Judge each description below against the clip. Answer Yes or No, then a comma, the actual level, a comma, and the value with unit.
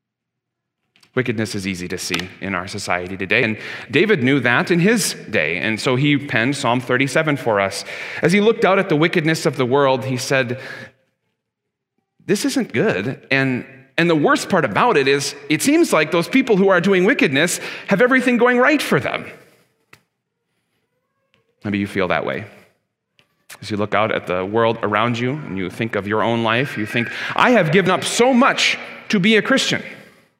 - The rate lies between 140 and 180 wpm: No, average, 190 wpm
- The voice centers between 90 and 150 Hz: Yes, low, 135 Hz